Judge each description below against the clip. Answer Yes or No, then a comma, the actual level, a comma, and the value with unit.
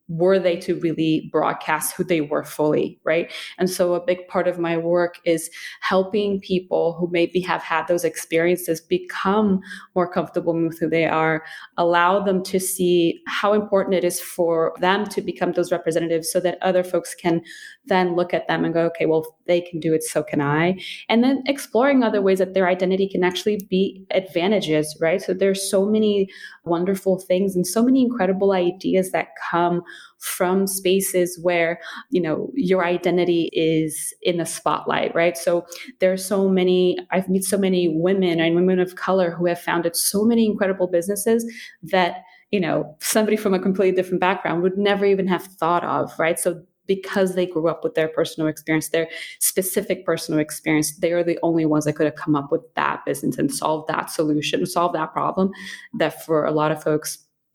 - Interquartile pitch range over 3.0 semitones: No, narrow, 2.4 semitones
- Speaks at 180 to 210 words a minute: Yes, average, 190 wpm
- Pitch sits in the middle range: Yes, medium, 180 Hz